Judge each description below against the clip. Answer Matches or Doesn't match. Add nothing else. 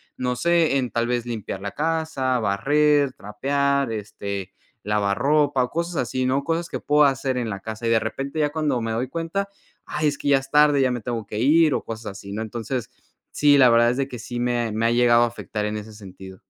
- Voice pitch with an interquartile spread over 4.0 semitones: Matches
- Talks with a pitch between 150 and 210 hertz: Doesn't match